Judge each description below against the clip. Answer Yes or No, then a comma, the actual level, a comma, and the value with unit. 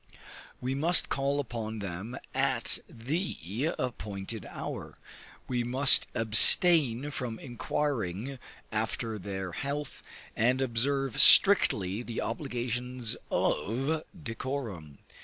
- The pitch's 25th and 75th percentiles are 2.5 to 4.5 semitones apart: Yes, average, 4.1 semitones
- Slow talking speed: Yes, slow, 95 wpm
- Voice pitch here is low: Yes, low, 120 Hz